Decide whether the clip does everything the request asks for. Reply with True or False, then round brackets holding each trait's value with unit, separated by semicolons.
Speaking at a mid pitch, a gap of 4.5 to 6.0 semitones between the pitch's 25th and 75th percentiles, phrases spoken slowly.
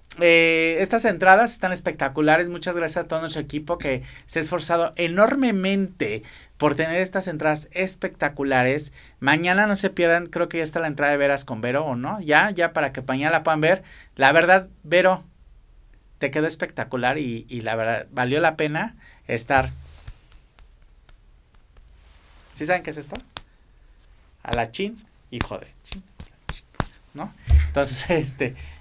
False (160 Hz; 5.1 semitones; 150 wpm)